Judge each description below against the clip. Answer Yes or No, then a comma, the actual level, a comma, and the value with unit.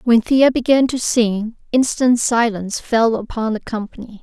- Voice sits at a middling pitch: No, high, 230 Hz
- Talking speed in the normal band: Yes, average, 155 wpm